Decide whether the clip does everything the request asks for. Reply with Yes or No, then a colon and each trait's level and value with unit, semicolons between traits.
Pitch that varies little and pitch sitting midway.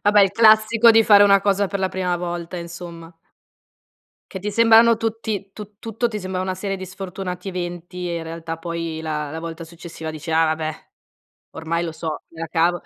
No: average, 3.5 semitones; medium, 180 Hz